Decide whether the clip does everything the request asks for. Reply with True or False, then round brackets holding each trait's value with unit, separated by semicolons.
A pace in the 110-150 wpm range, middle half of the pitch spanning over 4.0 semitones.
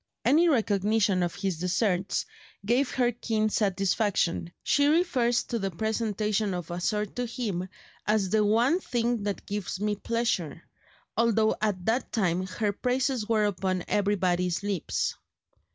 False (145 wpm; 3.6 semitones)